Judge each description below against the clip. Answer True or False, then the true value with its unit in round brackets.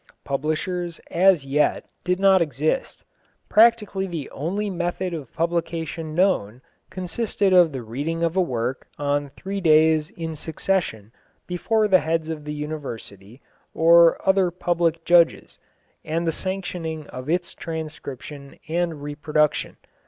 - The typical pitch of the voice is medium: True (165 Hz)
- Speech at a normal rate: False (130 wpm)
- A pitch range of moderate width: True (3.4 semitones)